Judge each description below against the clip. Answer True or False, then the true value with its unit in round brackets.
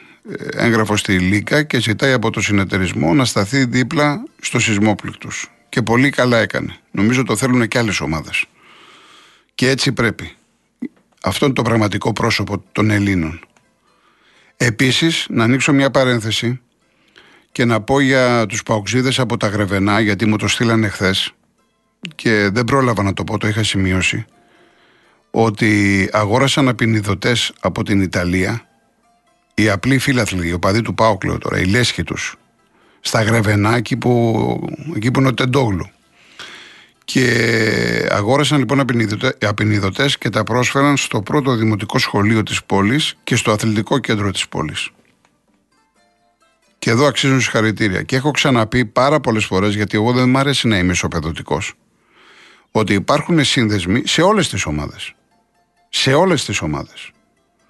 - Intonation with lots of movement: False (4.1 semitones)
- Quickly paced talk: False (140 wpm)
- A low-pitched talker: True (115 Hz)